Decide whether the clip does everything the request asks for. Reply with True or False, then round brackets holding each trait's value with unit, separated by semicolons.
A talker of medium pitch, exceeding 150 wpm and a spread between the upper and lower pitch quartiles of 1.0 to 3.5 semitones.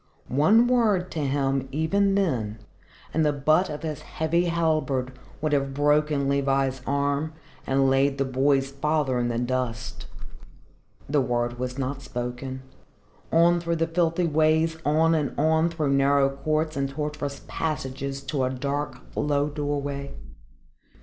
False (145 Hz; 145 wpm; 2.8 semitones)